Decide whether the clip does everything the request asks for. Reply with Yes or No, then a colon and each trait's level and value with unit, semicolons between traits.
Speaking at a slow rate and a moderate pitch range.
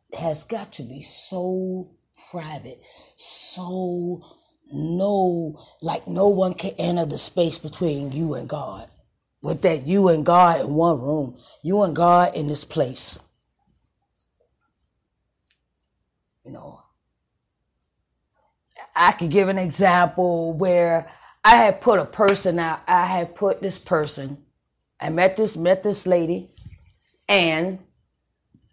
Yes: slow, 125 wpm; average, 3.4 semitones